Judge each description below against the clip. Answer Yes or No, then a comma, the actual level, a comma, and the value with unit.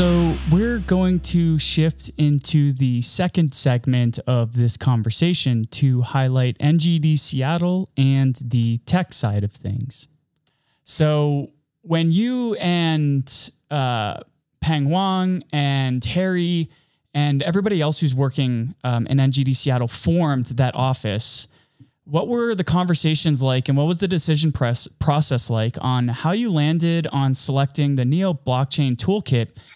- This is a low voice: No, medium, 145 Hz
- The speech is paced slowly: Yes, slow, 130 wpm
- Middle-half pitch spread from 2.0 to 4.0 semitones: No, average, 4.4 semitones